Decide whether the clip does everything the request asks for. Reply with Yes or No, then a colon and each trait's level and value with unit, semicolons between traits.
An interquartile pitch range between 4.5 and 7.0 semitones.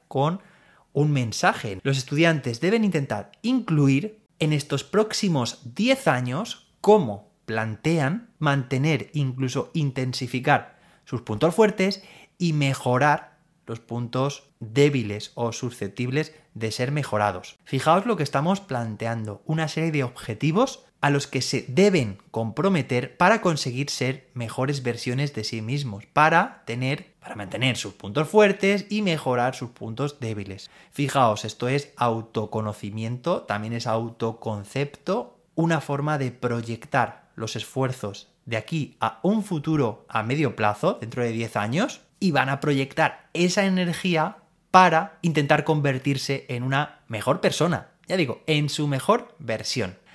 Yes: wide, 5.5 semitones